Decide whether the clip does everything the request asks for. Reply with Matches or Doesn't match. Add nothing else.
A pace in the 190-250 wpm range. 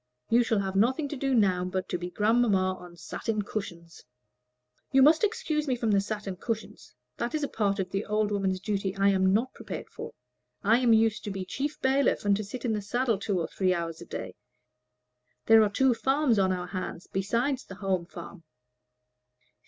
Matches